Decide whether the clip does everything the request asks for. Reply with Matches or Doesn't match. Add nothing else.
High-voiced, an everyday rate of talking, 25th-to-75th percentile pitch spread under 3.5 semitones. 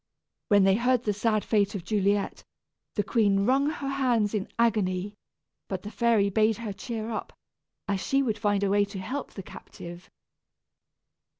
Matches